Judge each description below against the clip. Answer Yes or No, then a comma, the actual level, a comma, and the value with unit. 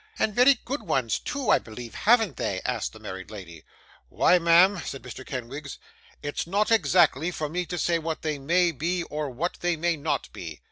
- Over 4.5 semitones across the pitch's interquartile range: Yes, average, 5.2 semitones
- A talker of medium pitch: Yes, medium, 165 Hz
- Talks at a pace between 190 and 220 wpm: Yes, average, 195 wpm